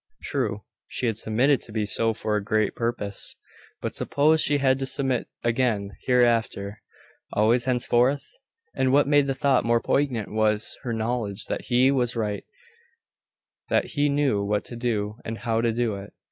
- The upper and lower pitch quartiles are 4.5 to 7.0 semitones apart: No, average, 3.4 semitones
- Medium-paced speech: Yes, average, 170 wpm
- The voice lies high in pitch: No, low, 120 Hz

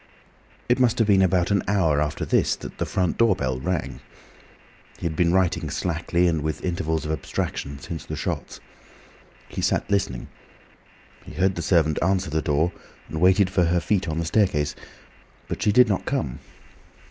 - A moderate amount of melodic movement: Yes, average, 3.5 semitones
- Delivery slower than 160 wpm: No, average, 180 wpm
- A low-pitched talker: Yes, very low, 85 Hz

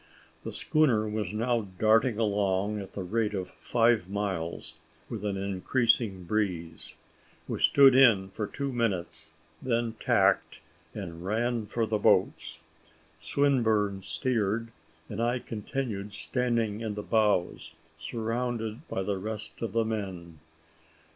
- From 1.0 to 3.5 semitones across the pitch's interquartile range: Yes, average, 3.0 semitones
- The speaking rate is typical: No, slow, 130 wpm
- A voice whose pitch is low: Yes, low, 110 Hz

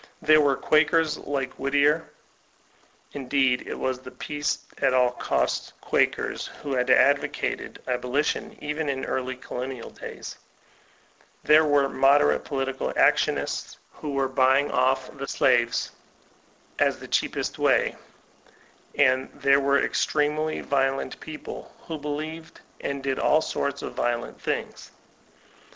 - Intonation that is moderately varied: No, narrow, 2.2 semitones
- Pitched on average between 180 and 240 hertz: No, medium, 140 Hz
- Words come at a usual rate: No, slow, 130 wpm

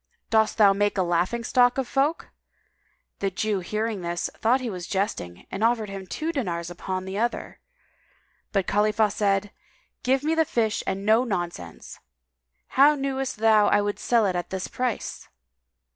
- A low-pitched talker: No, high, 210 Hz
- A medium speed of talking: Yes, average, 165 wpm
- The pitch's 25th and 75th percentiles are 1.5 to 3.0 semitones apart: No, average, 4.0 semitones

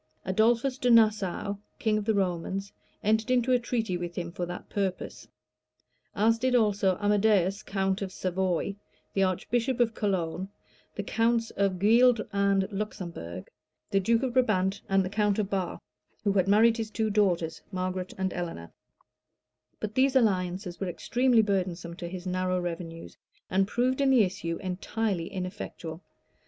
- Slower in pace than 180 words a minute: Yes, average, 150 wpm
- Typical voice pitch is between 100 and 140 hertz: No, high, 195 Hz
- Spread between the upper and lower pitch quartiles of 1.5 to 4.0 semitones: Yes, average, 3.4 semitones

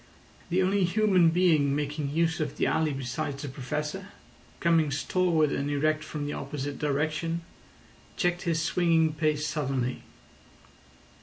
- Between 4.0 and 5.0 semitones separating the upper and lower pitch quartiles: No, average, 2.7 semitones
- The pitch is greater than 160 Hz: No, medium, 155 Hz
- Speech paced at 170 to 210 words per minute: No, slow, 135 wpm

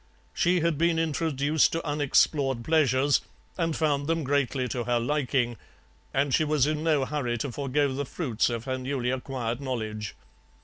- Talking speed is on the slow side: No, average, 165 wpm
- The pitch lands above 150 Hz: No, medium, 140 Hz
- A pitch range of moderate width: Yes, average, 3.3 semitones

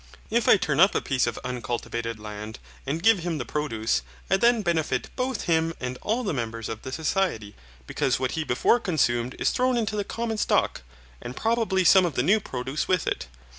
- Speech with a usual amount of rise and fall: No, wide, 8.7 semitones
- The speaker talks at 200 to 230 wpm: Yes, fast, 205 wpm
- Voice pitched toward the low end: No, medium, 155 Hz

